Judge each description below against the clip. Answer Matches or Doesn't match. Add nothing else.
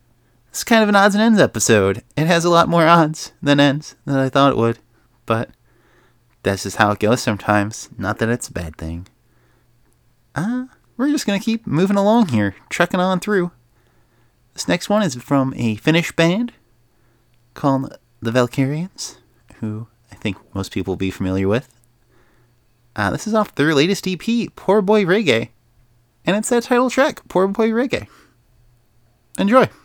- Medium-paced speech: Matches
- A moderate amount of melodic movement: Doesn't match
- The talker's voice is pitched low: Matches